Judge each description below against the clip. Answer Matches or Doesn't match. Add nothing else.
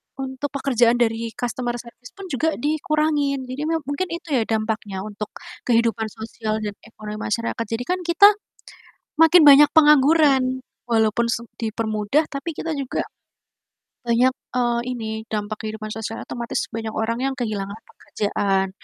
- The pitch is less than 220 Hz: Doesn't match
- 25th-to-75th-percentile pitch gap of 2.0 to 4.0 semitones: Doesn't match